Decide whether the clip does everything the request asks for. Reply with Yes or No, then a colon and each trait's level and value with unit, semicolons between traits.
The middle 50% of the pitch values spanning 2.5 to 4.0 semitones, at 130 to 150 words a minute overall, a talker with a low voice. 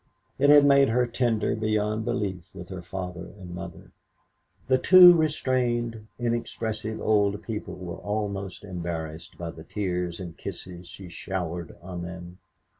No: average, 4.7 semitones; average, 145 wpm; low, 100 Hz